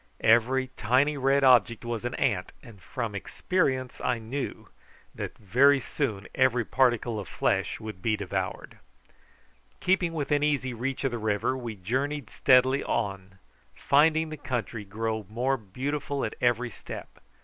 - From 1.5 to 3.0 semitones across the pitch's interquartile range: No, average, 3.8 semitones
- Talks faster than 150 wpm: No, average, 145 wpm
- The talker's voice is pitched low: Yes, low, 125 Hz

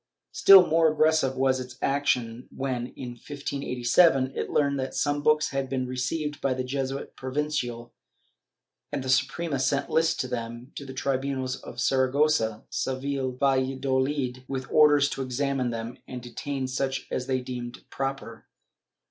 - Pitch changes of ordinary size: No, narrow, 1.8 semitones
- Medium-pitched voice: No, low, 130 Hz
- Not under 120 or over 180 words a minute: Yes, average, 150 wpm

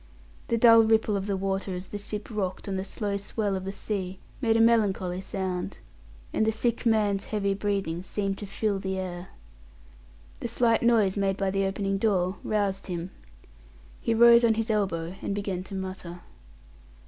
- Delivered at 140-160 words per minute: No, average, 180 wpm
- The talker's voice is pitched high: Yes, high, 200 Hz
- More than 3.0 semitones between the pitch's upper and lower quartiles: No, narrow, 2.4 semitones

